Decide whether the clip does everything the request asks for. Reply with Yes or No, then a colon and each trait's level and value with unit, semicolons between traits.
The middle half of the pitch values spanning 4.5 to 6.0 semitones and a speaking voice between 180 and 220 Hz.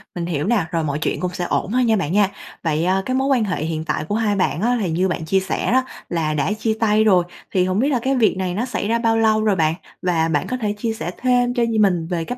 Yes: average, 5.1 semitones; high, 195 Hz